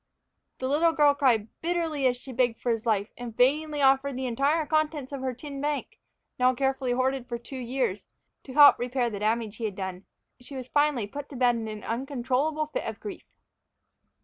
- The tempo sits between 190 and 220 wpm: Yes, average, 200 wpm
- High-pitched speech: Yes, very high, 260 Hz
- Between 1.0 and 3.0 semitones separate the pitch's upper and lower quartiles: No, average, 3.4 semitones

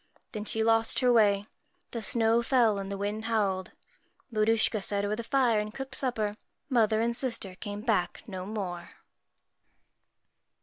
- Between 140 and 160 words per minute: Yes, average, 150 wpm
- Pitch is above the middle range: Yes, high, 220 Hz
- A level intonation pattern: Yes, narrow, 2.3 semitones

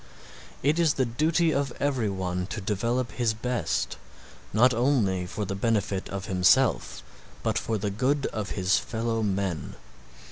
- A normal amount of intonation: Yes, average, 4.8 semitones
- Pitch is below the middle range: Yes, low, 110 Hz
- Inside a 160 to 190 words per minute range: No, average, 150 wpm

